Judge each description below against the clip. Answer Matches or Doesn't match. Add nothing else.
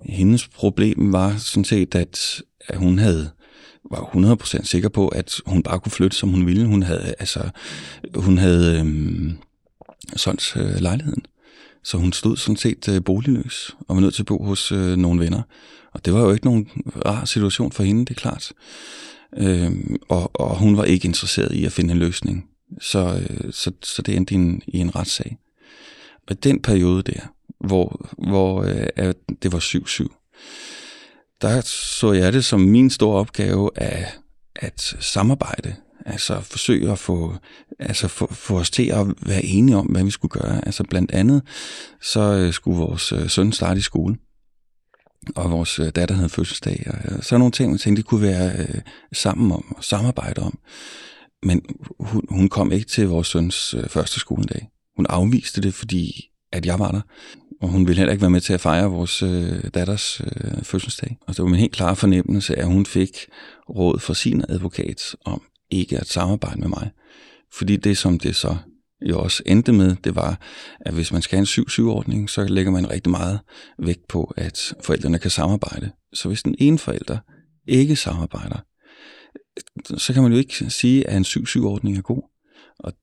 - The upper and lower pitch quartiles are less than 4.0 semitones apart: Matches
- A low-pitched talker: Matches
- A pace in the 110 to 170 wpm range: Doesn't match